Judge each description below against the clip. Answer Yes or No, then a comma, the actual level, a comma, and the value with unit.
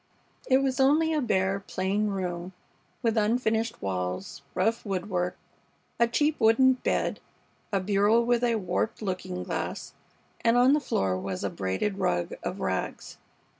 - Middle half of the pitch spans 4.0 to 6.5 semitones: Yes, average, 4.7 semitones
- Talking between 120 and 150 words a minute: Yes, average, 145 wpm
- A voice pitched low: No, high, 210 Hz